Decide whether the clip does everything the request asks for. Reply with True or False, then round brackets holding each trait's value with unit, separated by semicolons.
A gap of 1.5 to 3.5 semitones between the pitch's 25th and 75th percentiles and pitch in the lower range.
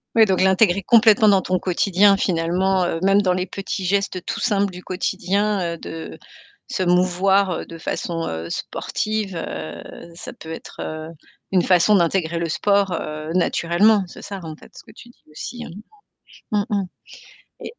False (2.8 semitones; 185 Hz)